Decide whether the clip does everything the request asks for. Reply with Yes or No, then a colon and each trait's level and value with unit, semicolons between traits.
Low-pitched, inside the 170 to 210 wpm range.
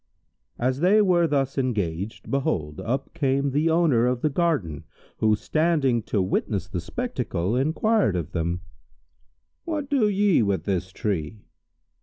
No: low, 130 Hz; average, 140 wpm